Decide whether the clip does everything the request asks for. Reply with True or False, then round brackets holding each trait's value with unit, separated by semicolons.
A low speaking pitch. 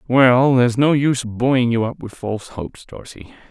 True (125 Hz)